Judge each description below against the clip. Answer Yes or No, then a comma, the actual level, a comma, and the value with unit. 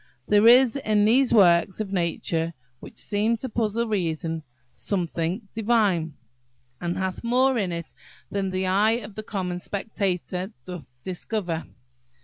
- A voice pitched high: Yes, high, 195 Hz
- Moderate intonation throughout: Yes, average, 3.9 semitones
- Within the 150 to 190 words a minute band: No, slow, 135 wpm